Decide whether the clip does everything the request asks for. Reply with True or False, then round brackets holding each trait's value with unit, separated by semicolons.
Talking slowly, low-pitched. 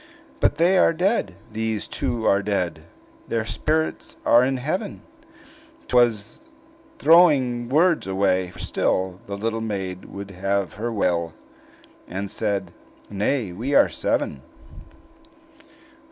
True (125 wpm; 110 Hz)